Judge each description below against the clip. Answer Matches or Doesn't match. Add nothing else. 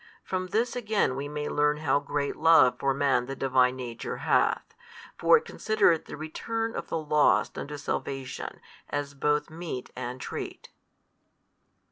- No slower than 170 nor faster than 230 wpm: Doesn't match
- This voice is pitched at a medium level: Matches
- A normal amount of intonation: Matches